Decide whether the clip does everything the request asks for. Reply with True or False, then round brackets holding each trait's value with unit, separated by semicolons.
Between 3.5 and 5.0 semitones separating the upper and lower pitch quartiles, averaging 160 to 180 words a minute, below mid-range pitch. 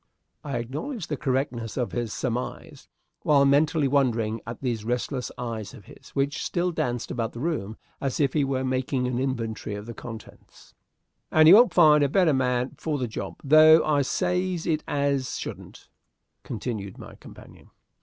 True (4.0 semitones; 170 wpm; 130 Hz)